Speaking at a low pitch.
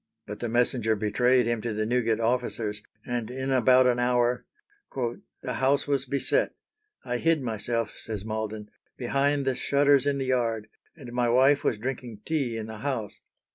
Yes: low, 120 Hz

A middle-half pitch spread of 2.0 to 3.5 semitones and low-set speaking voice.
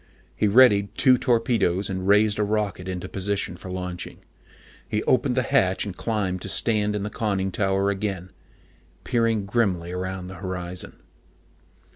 Yes: narrow, 2.6 semitones; low, 100 Hz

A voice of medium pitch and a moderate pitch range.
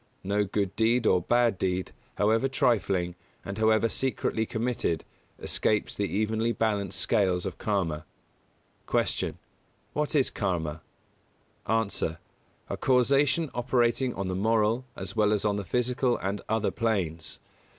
No: low, 110 Hz; average, 3.7 semitones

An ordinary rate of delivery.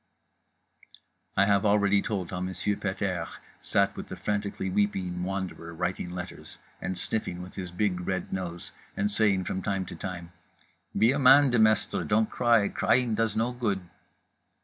Yes: average, 160 wpm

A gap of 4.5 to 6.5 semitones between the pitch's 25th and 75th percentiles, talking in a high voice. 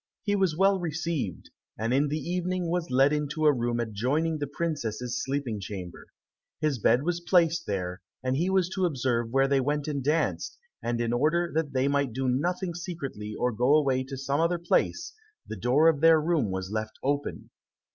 No: average, 5.1 semitones; medium, 140 Hz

